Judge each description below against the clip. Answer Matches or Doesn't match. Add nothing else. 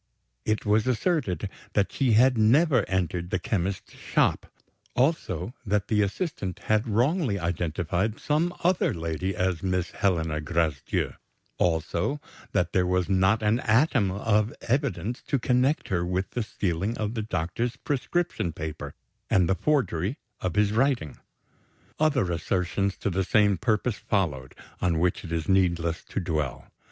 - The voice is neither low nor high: Doesn't match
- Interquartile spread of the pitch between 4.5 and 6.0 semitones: Matches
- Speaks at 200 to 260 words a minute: Doesn't match